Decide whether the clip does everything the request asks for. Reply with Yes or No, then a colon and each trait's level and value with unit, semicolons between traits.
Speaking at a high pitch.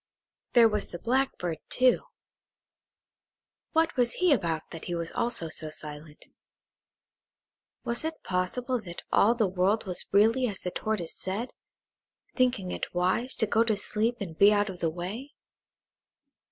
Yes: high, 205 Hz